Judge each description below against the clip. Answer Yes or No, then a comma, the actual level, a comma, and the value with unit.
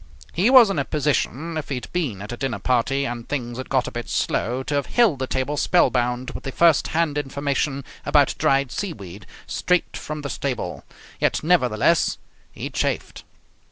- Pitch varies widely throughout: No, average, 3.8 semitones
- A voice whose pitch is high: No, medium, 140 Hz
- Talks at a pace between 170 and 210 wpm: Yes, average, 185 wpm